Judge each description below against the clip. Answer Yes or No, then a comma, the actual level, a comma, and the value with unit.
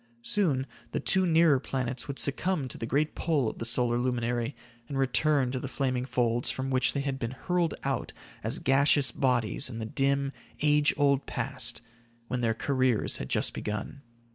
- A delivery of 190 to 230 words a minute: No, average, 180 wpm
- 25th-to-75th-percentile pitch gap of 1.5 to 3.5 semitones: Yes, narrow, 2.6 semitones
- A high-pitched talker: No, low, 135 Hz